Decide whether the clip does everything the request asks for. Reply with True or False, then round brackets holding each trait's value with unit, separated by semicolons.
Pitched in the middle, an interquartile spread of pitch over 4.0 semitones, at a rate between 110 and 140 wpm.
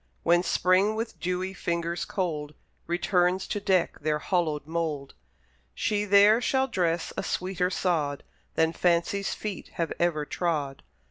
False (175 Hz; 2.8 semitones; 135 wpm)